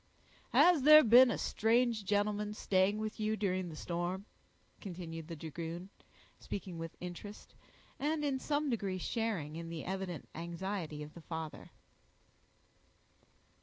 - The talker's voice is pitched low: No, high, 190 Hz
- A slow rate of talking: Yes, slow, 130 wpm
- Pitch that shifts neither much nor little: Yes, average, 4.5 semitones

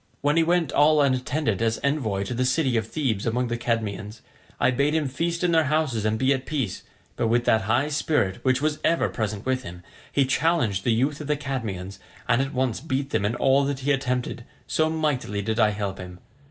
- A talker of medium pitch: No, low, 130 Hz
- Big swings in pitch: No, average, 4.9 semitones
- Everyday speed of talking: No, fast, 220 wpm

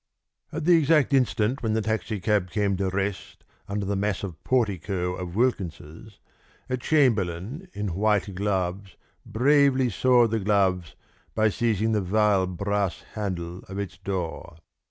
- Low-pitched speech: Yes, low, 100 Hz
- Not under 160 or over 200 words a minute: No, slow, 135 wpm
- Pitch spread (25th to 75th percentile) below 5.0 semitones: Yes, average, 3.3 semitones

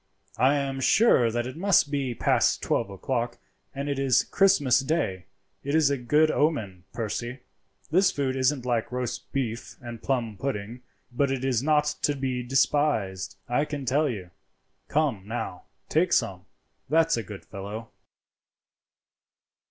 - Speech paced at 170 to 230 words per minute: No, average, 150 wpm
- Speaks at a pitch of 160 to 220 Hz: No, low, 130 Hz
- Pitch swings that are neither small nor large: Yes, average, 3.8 semitones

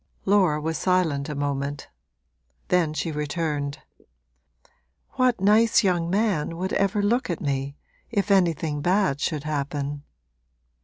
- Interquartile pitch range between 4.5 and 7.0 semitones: Yes, average, 5.0 semitones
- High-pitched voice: No, medium, 165 Hz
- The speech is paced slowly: Yes, slow, 120 wpm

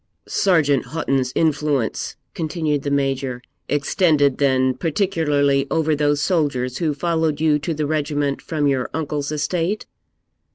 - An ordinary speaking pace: No, slow, 125 wpm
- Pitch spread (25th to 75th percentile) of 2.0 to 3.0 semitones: Yes, narrow, 2.4 semitones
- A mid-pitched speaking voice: Yes, medium, 145 Hz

